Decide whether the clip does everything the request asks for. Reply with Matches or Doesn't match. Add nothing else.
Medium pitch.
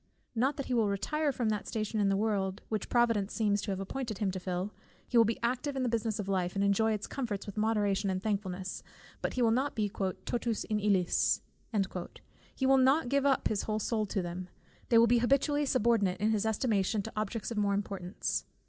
Doesn't match